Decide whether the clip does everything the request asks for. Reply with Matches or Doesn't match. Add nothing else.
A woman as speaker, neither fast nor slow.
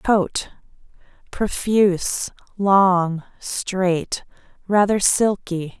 Doesn't match